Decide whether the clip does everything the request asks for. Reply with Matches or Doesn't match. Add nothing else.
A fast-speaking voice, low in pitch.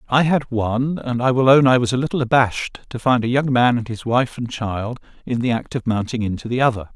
Matches